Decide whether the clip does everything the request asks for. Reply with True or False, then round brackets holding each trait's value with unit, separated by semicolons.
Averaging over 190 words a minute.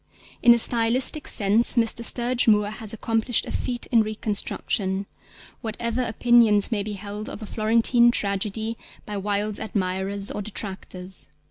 False (140 wpm)